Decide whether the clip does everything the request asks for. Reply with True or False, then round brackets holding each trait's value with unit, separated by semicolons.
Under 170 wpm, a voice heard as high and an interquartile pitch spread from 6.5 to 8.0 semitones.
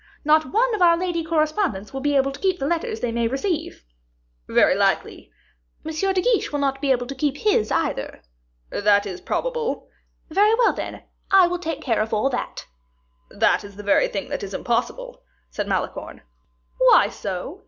False (185 wpm; 305 Hz; 7.6 semitones)